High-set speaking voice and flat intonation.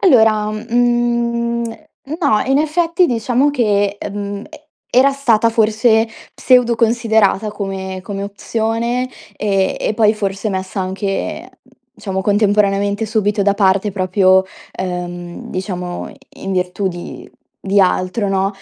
No: high, 210 Hz; average, 3.3 semitones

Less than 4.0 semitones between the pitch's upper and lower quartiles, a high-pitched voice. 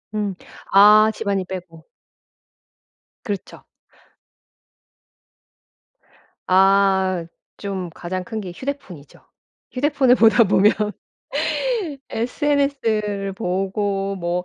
Yes: average, 2.8 semitones; high, 200 Hz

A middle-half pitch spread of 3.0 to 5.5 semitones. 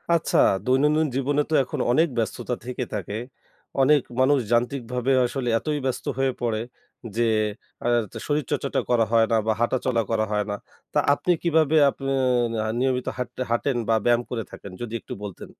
Yes: average, 3.3 semitones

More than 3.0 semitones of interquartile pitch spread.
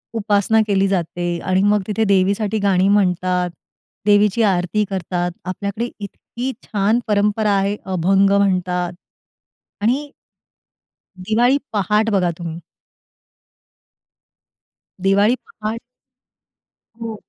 No: narrow, 2.4 semitones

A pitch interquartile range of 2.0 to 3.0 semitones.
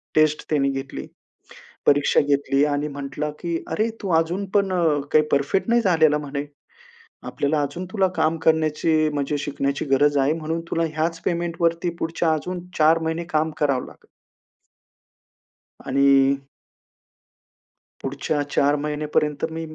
Yes: narrow, 2.5 semitones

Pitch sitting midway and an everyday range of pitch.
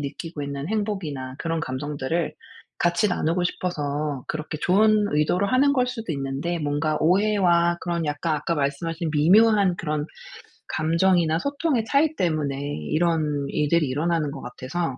Yes: medium, 165 Hz; average, 3.8 semitones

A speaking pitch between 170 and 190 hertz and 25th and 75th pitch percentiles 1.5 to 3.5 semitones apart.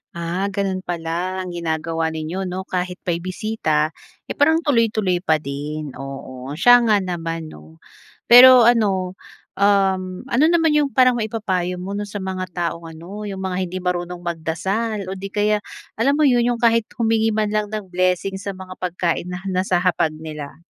No: medium, 185 Hz; average, 3.9 semitones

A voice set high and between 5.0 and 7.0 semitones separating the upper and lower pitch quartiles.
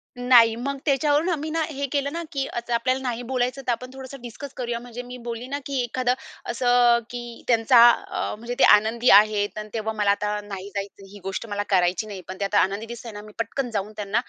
No: high, 235 Hz; average, 3.3 semitones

